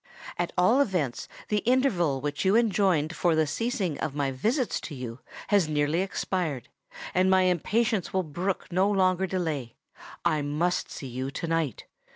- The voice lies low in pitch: No, medium, 175 Hz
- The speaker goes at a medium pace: Yes, average, 165 wpm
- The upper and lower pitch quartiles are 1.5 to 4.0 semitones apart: No, average, 4.7 semitones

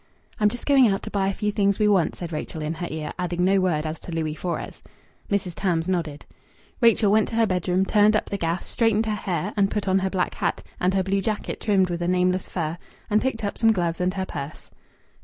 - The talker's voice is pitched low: No, high, 190 Hz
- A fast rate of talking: Yes, fast, 240 wpm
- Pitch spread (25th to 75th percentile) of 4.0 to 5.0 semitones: No, average, 3.2 semitones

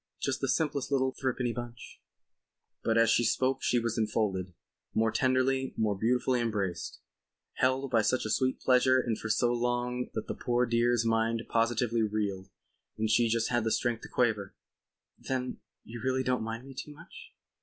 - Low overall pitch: Yes, low, 120 Hz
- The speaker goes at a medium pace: Yes, average, 170 wpm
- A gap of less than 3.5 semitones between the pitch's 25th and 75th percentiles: Yes, narrow, 2.4 semitones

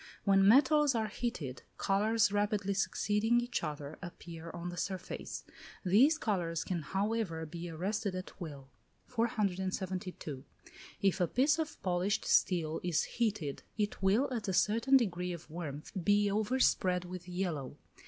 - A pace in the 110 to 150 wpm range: Yes, average, 140 wpm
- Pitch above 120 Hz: Yes, high, 190 Hz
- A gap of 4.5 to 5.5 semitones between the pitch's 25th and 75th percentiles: No, average, 3.9 semitones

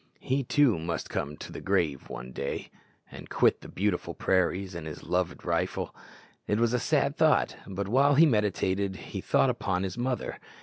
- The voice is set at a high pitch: No, low, 100 Hz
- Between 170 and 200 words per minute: Yes, average, 180 wpm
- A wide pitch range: Yes, wide, 5.8 semitones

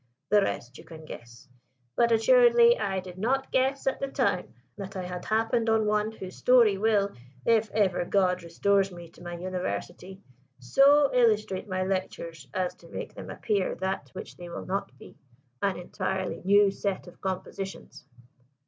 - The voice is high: Yes, high, 195 Hz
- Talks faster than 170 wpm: No, average, 165 wpm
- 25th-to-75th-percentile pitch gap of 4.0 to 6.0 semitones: No, average, 3.6 semitones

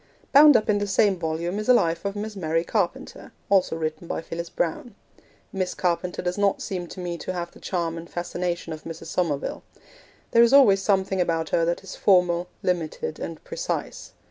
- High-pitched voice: No, medium, 180 Hz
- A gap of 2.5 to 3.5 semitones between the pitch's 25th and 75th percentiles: Yes, average, 3.1 semitones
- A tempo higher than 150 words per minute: Yes, average, 195 wpm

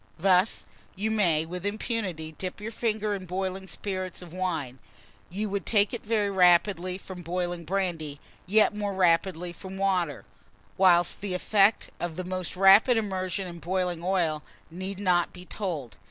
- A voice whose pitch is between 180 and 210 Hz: Yes, medium, 185 Hz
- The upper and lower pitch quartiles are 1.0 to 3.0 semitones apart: Yes, narrow, 2.4 semitones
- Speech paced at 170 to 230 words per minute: No, average, 155 wpm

